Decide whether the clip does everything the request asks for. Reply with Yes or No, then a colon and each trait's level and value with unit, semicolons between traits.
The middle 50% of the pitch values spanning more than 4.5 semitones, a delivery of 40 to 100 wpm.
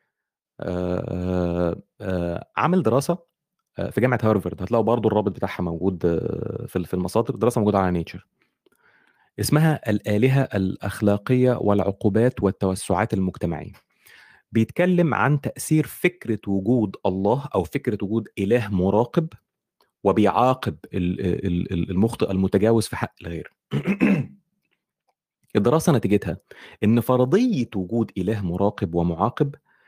Yes: average, 5.2 semitones; average, 95 wpm